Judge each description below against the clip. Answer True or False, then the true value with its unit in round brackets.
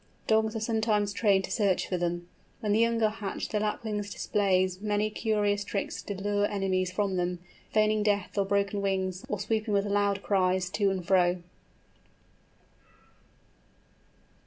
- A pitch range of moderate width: False (2.0 semitones)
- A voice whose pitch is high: True (205 Hz)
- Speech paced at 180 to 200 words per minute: False (155 wpm)